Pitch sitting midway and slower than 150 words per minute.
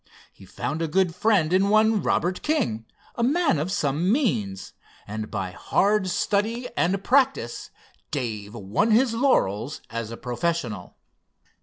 Yes: medium, 175 Hz; average, 140 wpm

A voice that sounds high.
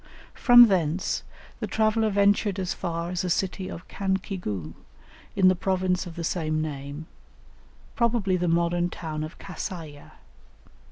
No: medium, 180 Hz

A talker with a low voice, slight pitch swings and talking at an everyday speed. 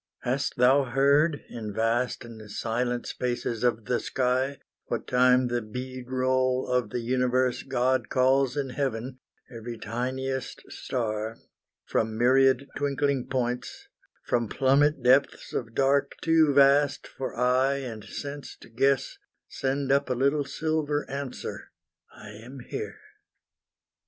No: low, 130 Hz; narrow, 2.2 semitones; slow, 130 wpm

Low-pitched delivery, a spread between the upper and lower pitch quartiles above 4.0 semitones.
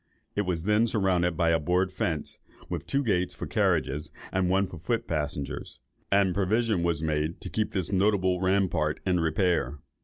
No: very low, 90 Hz; average, 3.1 semitones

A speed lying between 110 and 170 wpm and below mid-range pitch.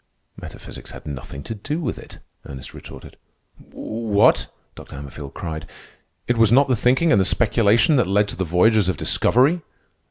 Yes: average, 165 wpm; low, 105 Hz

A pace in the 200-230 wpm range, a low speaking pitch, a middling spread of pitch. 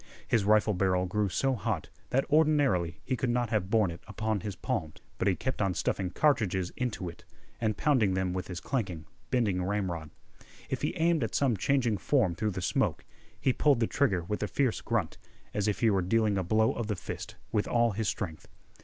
Yes: fast, 205 wpm; low, 105 Hz; average, 4.5 semitones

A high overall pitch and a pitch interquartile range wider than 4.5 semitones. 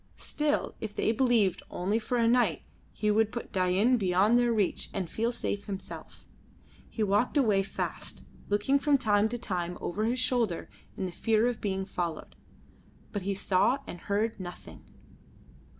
No: high, 210 Hz; average, 3.8 semitones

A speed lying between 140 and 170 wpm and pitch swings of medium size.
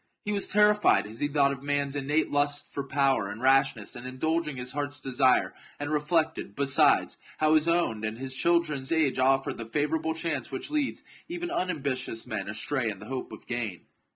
No: average, 185 wpm; average, 3.6 semitones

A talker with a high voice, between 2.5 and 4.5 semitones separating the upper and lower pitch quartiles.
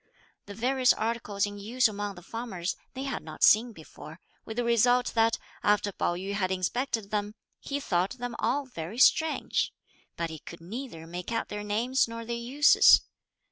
Yes: high, 220 Hz; average, 3.9 semitones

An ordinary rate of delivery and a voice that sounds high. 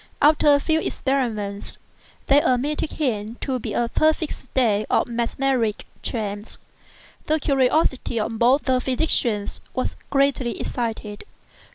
No: slow, 130 wpm; very high, 255 Hz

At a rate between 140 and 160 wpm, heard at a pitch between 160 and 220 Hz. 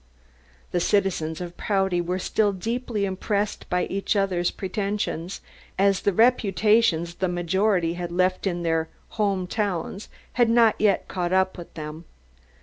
Yes: average, 145 wpm; high, 190 Hz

